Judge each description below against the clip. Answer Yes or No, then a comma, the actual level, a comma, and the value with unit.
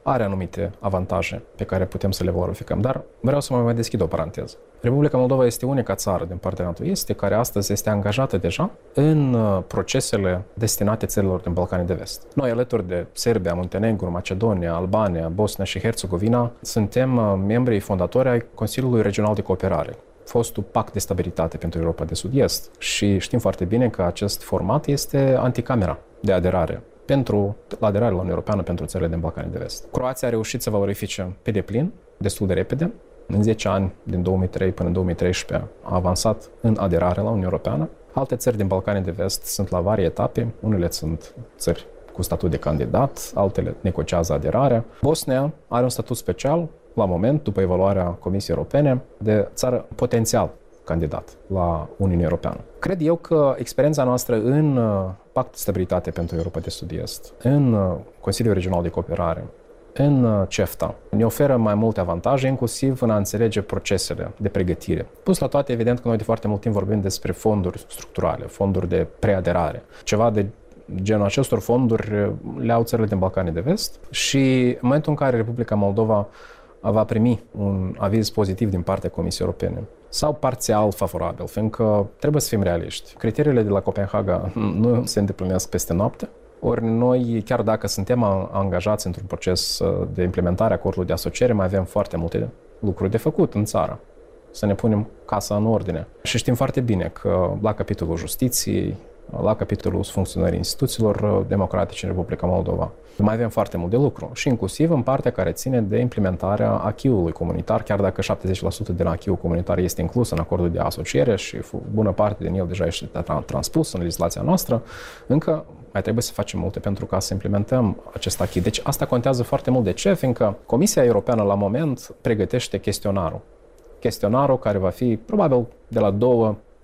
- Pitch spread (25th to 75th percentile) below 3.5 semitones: No, average, 4.4 semitones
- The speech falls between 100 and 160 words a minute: No, fast, 170 wpm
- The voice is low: Yes, low, 105 Hz